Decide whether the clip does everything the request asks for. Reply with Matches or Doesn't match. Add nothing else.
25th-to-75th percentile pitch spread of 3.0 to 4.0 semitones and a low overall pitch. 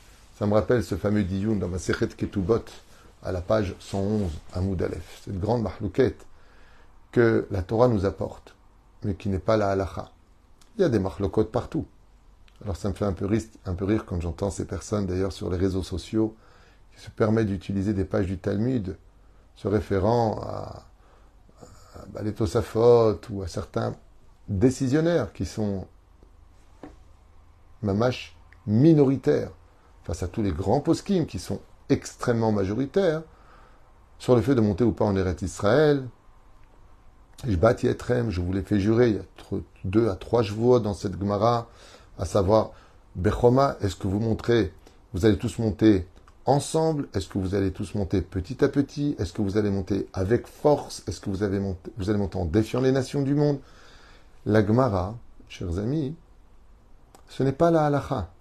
Matches